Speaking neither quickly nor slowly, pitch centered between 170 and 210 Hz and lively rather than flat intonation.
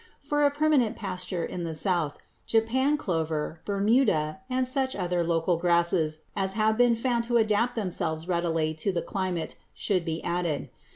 Yes: average, 160 wpm; medium, 185 Hz; wide, 5.9 semitones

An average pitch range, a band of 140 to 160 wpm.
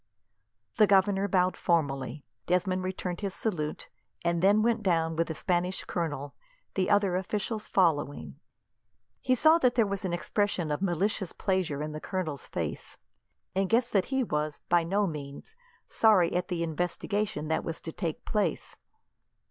Yes: average, 3.8 semitones; average, 155 wpm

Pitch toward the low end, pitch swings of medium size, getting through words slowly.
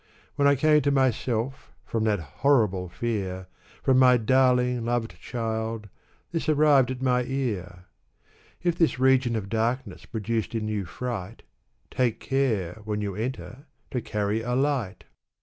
No: low, 120 Hz; average, 3.8 semitones; average, 150 wpm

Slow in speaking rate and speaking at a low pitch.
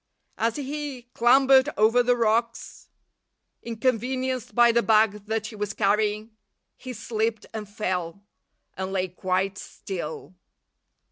No: slow, 120 wpm; high, 220 Hz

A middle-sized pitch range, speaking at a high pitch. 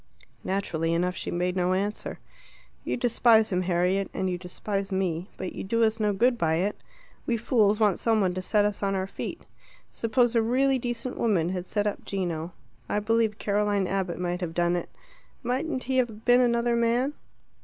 Yes: average, 4.2 semitones; high, 205 Hz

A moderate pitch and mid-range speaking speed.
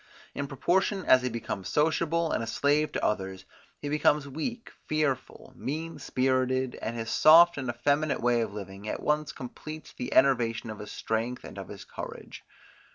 No: low, 130 Hz; average, 170 wpm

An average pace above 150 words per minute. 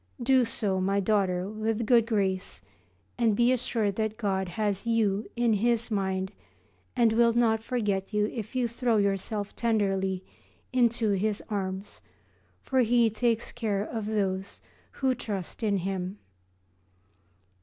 No: average, 140 wpm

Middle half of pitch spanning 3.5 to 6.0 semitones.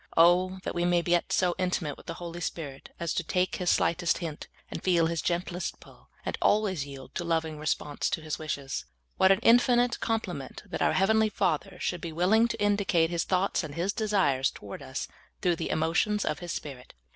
No: average, 3.1 semitones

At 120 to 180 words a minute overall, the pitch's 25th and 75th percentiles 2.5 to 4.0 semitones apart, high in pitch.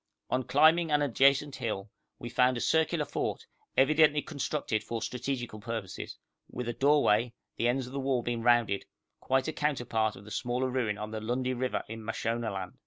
No: average, 175 wpm; average, 3.3 semitones; low, 125 Hz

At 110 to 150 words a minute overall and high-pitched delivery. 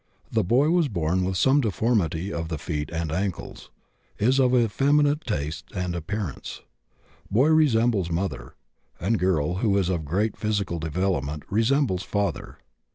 No: average, 145 wpm; very low, 95 Hz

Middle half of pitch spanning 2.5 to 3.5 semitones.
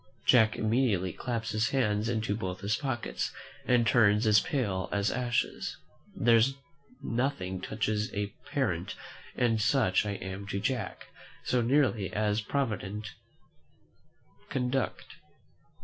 Yes: average, 3.1 semitones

